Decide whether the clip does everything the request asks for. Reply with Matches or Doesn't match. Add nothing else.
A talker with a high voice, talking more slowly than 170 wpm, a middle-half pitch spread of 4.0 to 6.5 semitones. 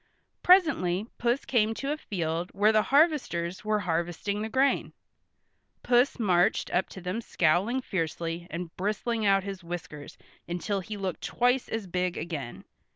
Matches